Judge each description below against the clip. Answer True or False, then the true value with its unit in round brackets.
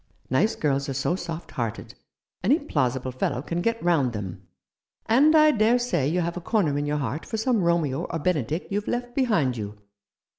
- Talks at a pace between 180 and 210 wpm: True (190 wpm)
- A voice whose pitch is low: False (165 Hz)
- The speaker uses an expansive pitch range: True (8.6 semitones)